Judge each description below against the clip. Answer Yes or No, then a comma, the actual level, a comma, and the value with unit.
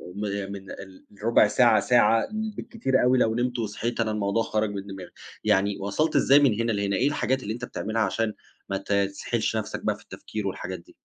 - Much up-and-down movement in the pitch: No, average, 3.5 semitones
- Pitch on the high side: No, low, 110 Hz